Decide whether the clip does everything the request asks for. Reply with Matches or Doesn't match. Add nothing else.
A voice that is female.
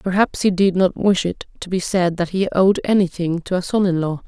Matches